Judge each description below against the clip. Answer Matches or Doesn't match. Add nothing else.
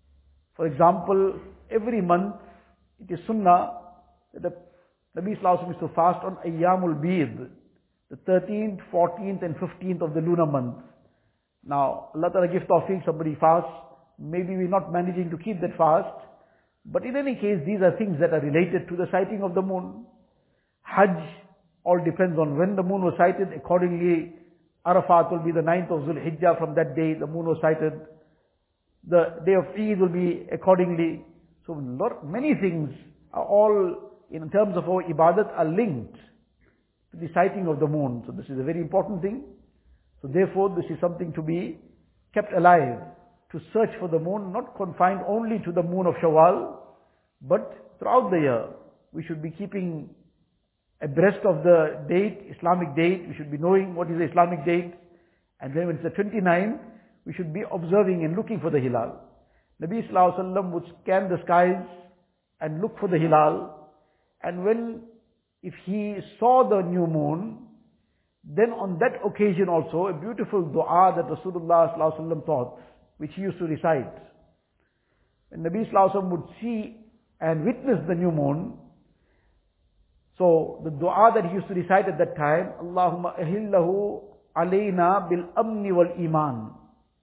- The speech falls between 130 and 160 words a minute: Doesn't match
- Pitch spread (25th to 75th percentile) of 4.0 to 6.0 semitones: Doesn't match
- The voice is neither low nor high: Matches